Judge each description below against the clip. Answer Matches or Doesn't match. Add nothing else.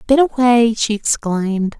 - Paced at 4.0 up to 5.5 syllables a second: Matches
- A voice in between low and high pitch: Doesn't match